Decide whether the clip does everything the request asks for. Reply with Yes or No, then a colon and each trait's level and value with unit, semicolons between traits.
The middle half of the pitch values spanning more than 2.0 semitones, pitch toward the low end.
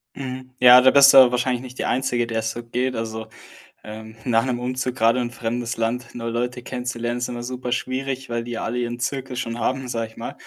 No: narrow, 1.6 semitones; low, 120 Hz